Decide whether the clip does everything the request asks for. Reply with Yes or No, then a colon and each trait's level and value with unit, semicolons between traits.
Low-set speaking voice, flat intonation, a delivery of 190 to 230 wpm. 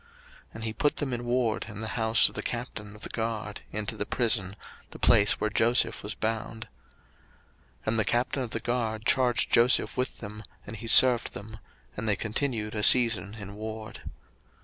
Yes: low, 110 Hz; narrow, 2.1 semitones; average, 195 wpm